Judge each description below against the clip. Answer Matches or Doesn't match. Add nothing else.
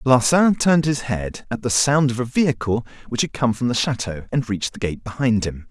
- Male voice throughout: Matches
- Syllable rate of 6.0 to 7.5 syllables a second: Doesn't match